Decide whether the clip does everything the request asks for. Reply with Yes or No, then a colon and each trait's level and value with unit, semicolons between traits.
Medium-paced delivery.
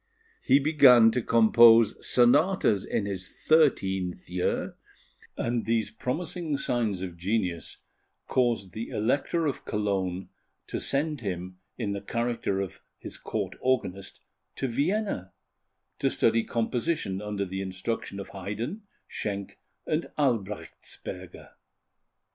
No: slow, 115 wpm